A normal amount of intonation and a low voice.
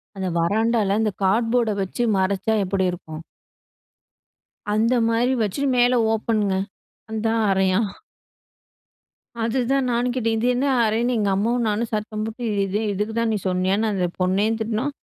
No: average, 3.1 semitones; high, 220 Hz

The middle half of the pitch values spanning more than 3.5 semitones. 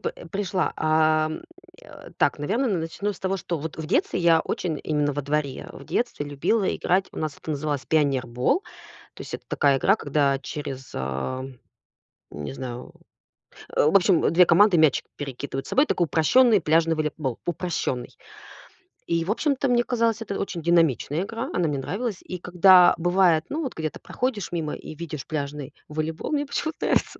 Yes: average, 4.9 semitones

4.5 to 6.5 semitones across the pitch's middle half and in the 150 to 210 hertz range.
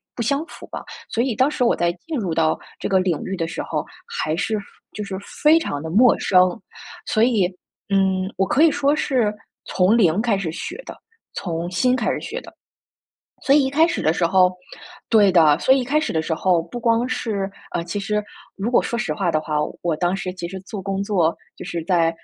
Yes: wide, 5.4 semitones; high, 195 Hz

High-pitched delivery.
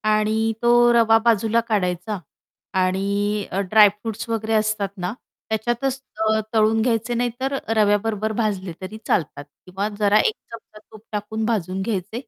Yes: high, 215 Hz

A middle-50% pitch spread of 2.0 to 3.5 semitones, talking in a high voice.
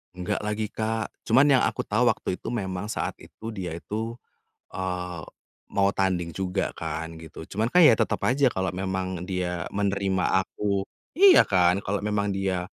No: average, 3.1 semitones; very low, 95 Hz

